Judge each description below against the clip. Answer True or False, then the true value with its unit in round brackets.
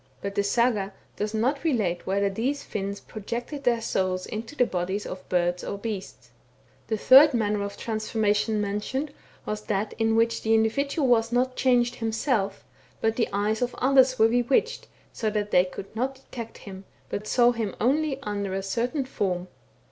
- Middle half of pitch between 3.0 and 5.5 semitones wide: True (3.6 semitones)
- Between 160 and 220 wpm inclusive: True (170 wpm)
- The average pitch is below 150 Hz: False (220 Hz)